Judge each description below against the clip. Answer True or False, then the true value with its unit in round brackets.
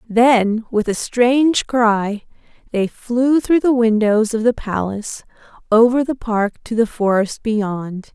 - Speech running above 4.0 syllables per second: False (3.7 syllables/s)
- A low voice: False (225 Hz)